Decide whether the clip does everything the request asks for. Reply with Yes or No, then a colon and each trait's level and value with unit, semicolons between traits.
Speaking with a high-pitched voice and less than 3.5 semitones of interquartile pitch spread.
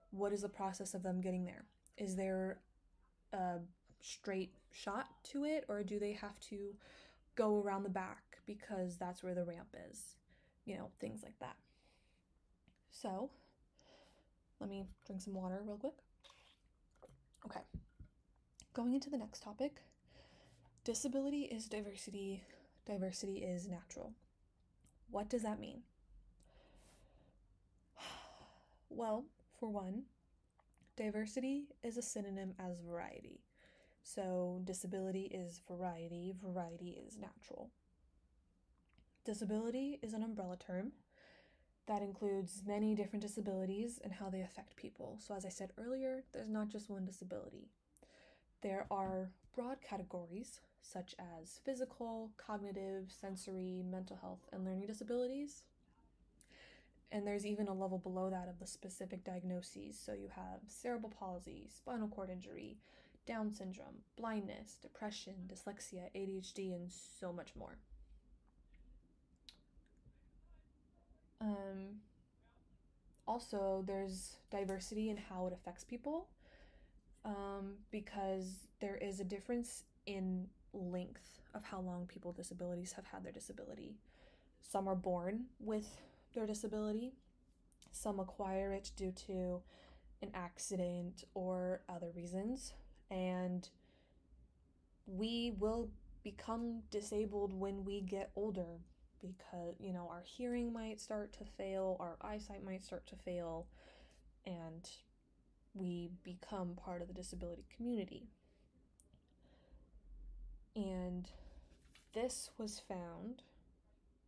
Yes: high, 195 Hz; average, 3.0 semitones